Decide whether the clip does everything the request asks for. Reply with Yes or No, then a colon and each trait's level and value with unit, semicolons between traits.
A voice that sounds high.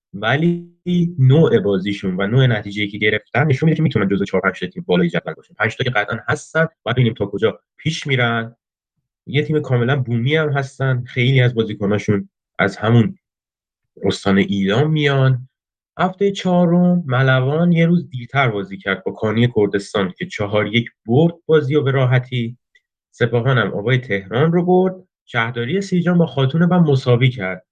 No: low, 130 Hz